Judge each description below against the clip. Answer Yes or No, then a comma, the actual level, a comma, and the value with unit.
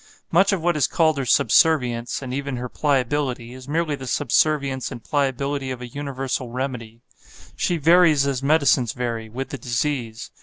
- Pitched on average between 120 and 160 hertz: Yes, low, 135 Hz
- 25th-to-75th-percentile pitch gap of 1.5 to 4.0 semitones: Yes, average, 3.1 semitones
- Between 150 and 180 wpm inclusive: Yes, average, 165 wpm